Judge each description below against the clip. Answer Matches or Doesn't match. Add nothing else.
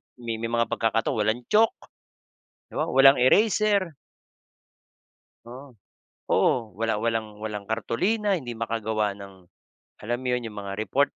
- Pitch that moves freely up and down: Doesn't match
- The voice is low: Matches